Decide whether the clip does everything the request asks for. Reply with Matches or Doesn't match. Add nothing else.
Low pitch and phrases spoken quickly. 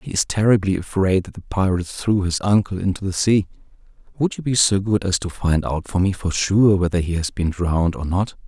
Matches